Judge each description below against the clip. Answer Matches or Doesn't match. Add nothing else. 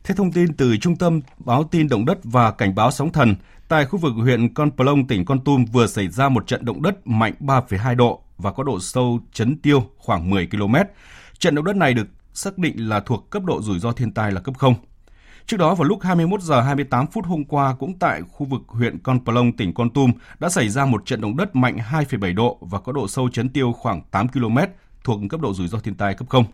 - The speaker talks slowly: Doesn't match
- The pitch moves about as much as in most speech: Matches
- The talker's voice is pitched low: Matches